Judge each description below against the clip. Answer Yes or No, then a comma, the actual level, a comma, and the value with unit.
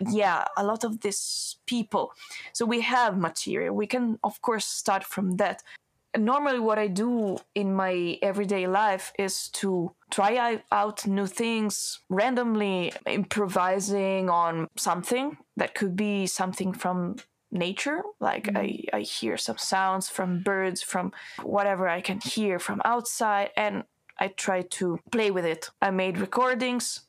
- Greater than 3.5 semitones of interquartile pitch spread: No, average, 2.8 semitones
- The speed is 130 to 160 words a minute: Yes, average, 150 wpm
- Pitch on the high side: Yes, high, 200 Hz